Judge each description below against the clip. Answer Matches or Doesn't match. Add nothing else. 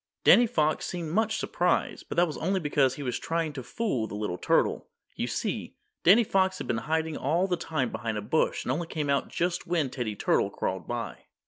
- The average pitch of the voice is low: Doesn't match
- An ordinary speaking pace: Doesn't match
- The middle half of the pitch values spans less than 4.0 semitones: Doesn't match